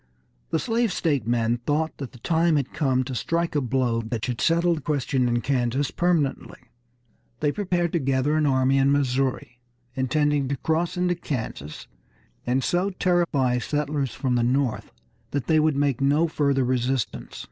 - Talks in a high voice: No, medium, 140 Hz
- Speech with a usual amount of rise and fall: Yes, average, 3.8 semitones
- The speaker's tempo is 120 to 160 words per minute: No, average, 170 wpm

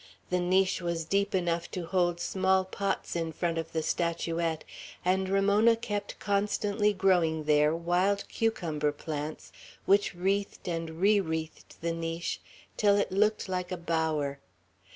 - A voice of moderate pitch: Yes, medium, 180 Hz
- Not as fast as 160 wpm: Yes, average, 145 wpm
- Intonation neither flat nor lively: Yes, average, 3.2 semitones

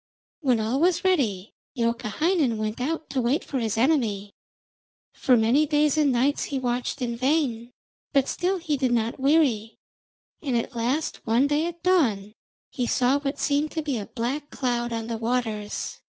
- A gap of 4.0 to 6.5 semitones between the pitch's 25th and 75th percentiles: Yes, average, 4.3 semitones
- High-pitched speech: Yes, very high, 255 Hz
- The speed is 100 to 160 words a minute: No, average, 170 wpm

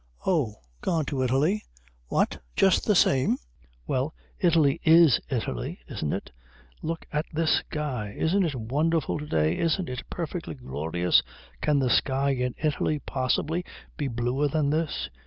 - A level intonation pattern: No, average, 4.3 semitones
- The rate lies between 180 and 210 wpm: No, average, 145 wpm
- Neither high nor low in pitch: Yes, medium, 145 Hz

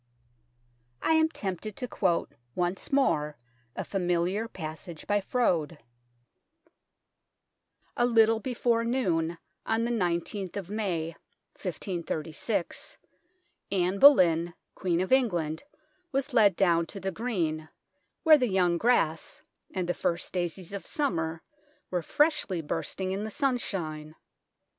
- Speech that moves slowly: Yes, slow, 120 wpm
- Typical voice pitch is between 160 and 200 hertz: Yes, high, 190 Hz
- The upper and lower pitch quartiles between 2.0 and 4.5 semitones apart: No, average, 5.3 semitones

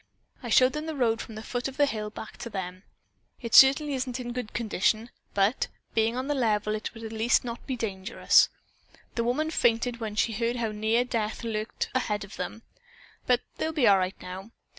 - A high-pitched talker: Yes, high, 230 Hz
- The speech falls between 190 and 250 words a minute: Yes, fast, 205 wpm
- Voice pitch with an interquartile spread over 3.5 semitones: No, average, 2.8 semitones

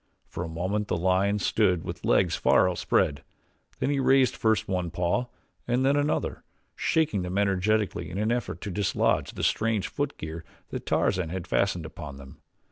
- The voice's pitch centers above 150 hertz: No, very low, 95 Hz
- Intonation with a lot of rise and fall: No, average, 4.0 semitones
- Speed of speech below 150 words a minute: No, average, 170 wpm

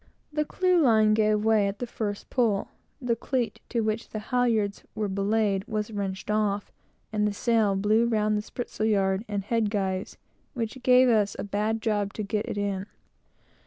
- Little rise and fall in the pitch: Yes, narrow, 2.0 semitones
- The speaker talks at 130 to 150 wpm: No, average, 175 wpm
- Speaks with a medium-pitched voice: No, high, 215 Hz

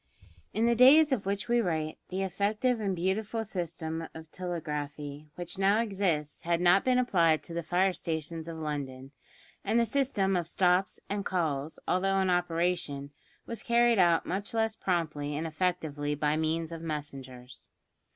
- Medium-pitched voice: Yes, medium, 175 Hz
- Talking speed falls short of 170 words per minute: Yes, average, 160 wpm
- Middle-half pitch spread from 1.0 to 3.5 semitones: No, average, 4.2 semitones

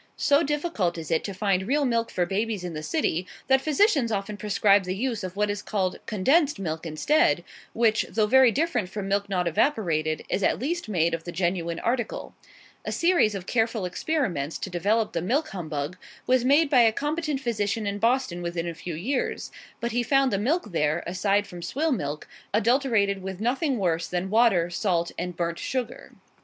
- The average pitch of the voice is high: Yes, high, 205 Hz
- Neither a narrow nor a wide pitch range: No, wide, 6.3 semitones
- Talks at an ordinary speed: Yes, average, 190 wpm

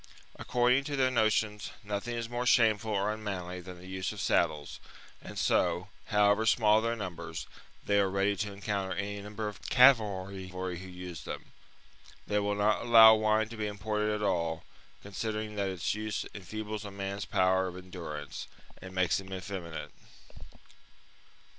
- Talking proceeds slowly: No, average, 160 wpm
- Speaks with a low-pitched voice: Yes, low, 100 Hz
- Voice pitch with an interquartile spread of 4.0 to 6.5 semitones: No, narrow, 2.6 semitones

